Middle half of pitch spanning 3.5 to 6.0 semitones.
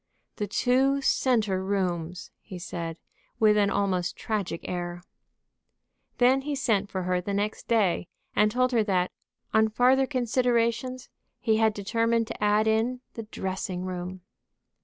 Yes: average, 4.4 semitones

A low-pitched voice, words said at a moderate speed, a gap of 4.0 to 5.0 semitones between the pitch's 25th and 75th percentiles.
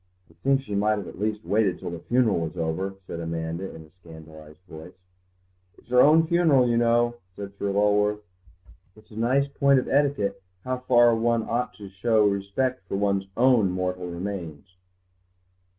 Yes: low, 105 Hz; average, 175 wpm; average, 4.7 semitones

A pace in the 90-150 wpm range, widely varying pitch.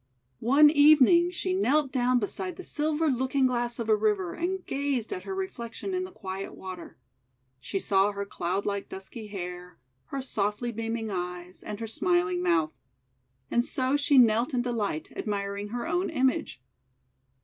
No: average, 170 wpm; wide, 6.3 semitones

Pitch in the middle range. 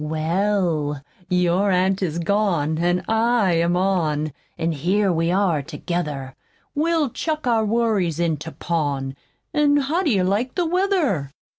Yes: medium, 180 Hz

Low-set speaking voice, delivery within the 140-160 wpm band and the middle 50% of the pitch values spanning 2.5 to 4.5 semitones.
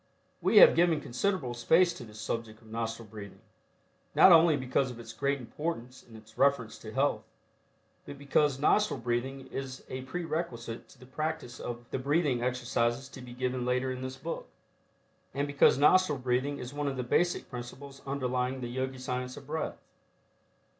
No: low, 130 Hz; average, 175 wpm; average, 2.9 semitones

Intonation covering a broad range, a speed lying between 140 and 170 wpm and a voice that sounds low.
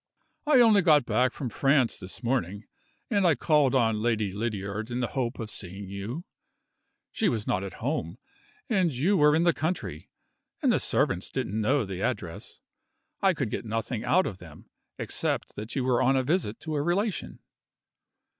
No: wide, 7.0 semitones; average, 180 wpm; low, 125 Hz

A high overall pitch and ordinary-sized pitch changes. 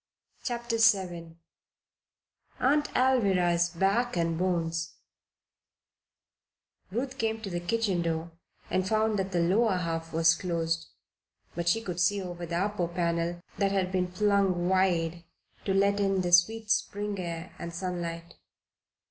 No: medium, 180 Hz; average, 3.2 semitones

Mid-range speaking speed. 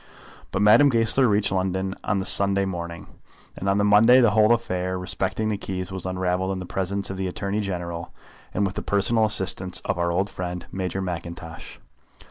Yes: average, 190 wpm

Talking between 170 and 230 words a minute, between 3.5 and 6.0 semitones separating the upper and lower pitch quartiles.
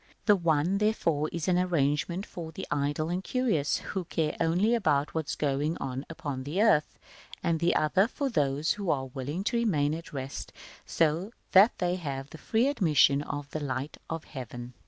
Yes: average, 175 wpm; average, 4.4 semitones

